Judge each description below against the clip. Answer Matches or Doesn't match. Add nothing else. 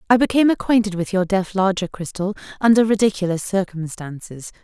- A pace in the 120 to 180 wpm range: Matches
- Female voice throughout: Matches